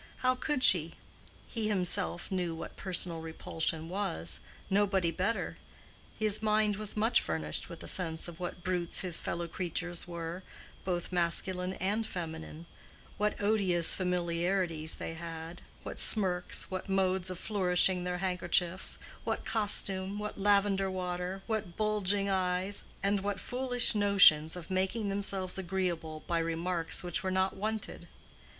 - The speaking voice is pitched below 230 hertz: Yes, medium, 185 Hz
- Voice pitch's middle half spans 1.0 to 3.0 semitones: Yes, average, 2.7 semitones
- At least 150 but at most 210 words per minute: No, slow, 135 wpm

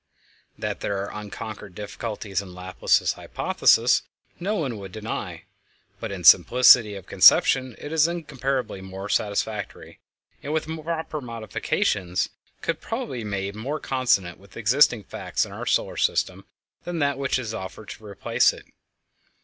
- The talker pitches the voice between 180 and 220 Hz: No, low, 110 Hz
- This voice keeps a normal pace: Yes, average, 150 wpm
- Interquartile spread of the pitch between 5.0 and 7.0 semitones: Yes, wide, 5.5 semitones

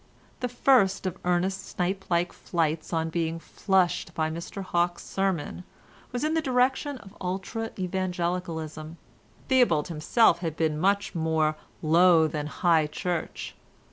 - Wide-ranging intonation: No, average, 3.2 semitones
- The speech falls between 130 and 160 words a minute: Yes, slow, 135 wpm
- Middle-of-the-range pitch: Yes, medium, 175 Hz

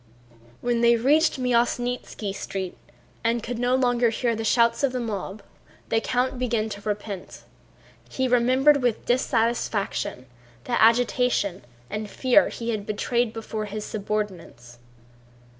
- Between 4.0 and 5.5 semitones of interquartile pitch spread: No, average, 2.7 semitones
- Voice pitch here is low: No, high, 235 Hz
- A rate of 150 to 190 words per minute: No, slow, 135 wpm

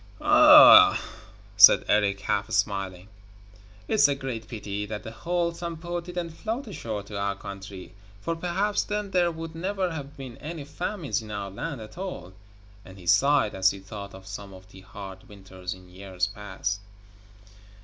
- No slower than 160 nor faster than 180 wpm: Yes, average, 165 wpm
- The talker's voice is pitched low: Yes, low, 110 Hz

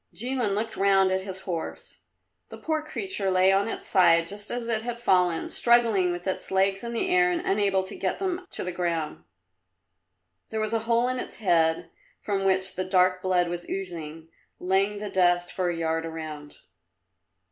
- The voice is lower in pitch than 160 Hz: No, high, 190 Hz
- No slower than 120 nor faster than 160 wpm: No, average, 185 wpm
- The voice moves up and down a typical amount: Yes, average, 4.0 semitones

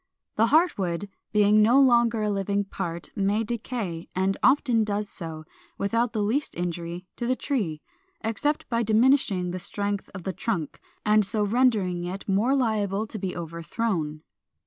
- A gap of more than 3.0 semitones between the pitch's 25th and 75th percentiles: Yes, average, 4.0 semitones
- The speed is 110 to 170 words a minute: Yes, average, 160 wpm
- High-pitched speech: Yes, high, 205 Hz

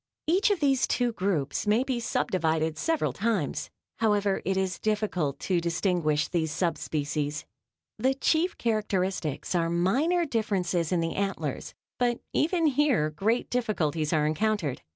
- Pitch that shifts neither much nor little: No, wide, 6.8 semitones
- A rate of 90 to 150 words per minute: Yes, average, 145 wpm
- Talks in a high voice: Yes, high, 195 Hz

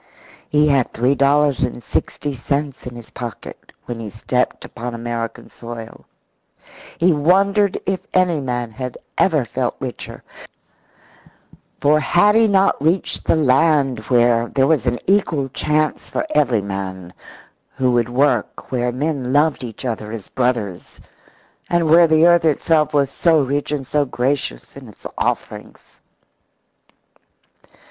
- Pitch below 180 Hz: Yes, low, 135 Hz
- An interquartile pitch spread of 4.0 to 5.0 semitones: Yes, average, 4.3 semitones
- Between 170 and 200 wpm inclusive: No, average, 140 wpm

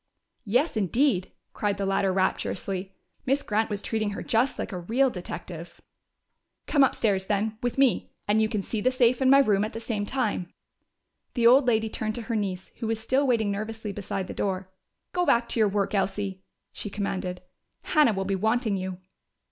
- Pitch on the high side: Yes, high, 215 Hz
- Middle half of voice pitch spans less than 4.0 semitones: Yes, average, 3.4 semitones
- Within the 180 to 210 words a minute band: Yes, average, 190 wpm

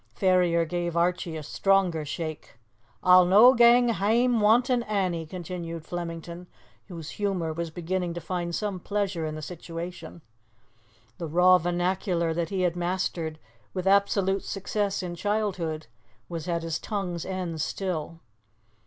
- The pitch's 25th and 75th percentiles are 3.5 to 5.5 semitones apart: No, average, 2.7 semitones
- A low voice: No, medium, 180 Hz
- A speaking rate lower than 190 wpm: Yes, slow, 135 wpm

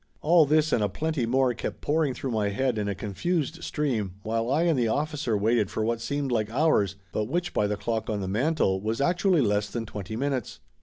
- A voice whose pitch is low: Yes, low, 120 Hz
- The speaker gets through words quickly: Yes, fast, 220 wpm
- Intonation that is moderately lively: No, wide, 6.1 semitones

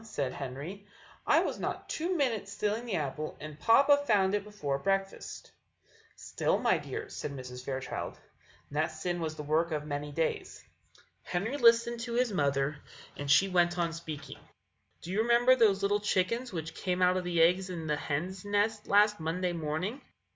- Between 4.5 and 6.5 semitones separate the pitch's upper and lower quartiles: Yes, wide, 5.5 semitones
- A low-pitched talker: No, medium, 180 Hz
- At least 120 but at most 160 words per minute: No, average, 175 wpm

